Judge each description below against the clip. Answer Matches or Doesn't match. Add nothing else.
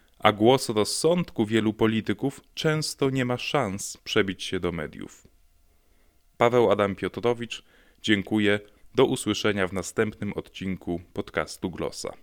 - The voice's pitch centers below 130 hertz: Matches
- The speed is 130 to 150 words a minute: Doesn't match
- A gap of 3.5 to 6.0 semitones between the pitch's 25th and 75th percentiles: Matches